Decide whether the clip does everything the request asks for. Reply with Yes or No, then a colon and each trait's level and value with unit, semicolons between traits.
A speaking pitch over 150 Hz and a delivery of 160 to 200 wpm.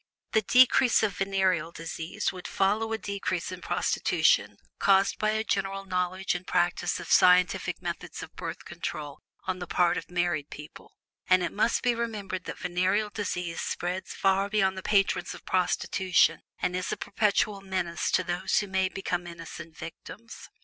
Yes: high, 190 Hz; average, 165 wpm